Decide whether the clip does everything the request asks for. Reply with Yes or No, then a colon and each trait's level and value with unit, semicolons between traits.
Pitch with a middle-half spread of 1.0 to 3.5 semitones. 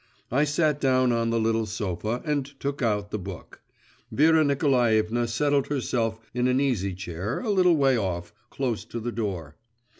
No: average, 4.5 semitones